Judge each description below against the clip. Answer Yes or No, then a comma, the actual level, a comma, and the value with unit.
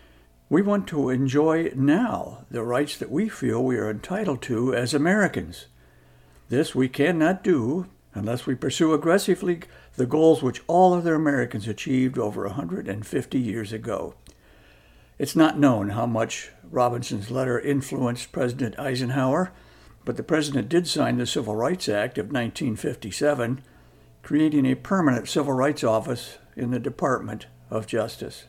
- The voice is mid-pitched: No, low, 130 Hz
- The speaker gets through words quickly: No, average, 140 wpm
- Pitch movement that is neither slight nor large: Yes, average, 4.8 semitones